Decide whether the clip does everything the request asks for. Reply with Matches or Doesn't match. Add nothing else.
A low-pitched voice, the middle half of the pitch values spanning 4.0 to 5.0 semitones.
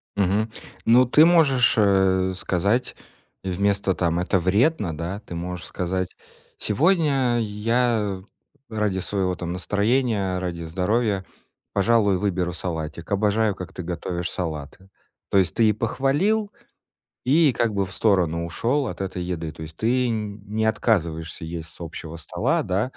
Matches